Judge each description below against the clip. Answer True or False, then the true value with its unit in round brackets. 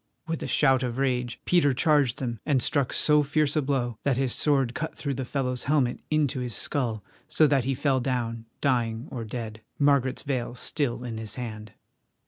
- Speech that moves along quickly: False (190 wpm)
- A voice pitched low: True (130 Hz)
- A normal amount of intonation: True (3.0 semitones)